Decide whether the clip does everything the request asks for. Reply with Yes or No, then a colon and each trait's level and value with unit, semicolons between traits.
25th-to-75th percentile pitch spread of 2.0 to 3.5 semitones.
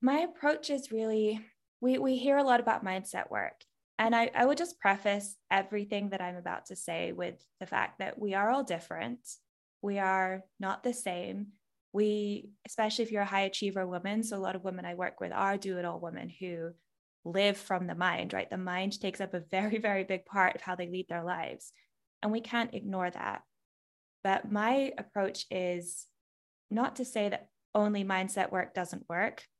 Yes: average, 3.0 semitones